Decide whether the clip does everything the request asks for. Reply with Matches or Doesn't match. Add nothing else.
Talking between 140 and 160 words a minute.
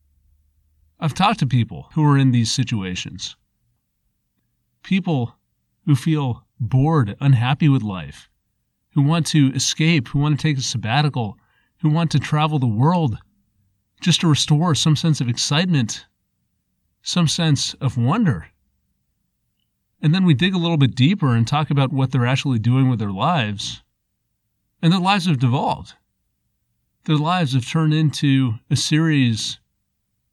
Matches